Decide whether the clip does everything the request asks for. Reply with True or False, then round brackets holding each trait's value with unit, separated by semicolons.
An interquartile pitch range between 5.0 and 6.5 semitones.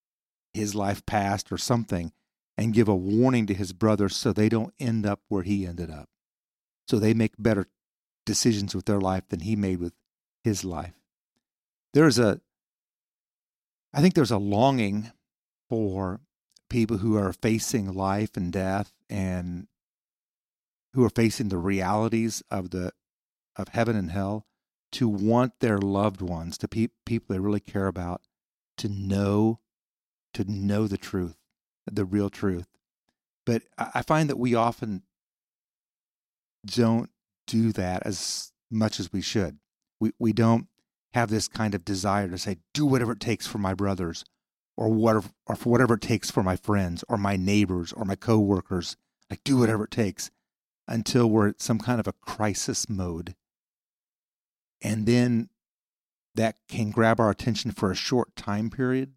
False (2.8 semitones)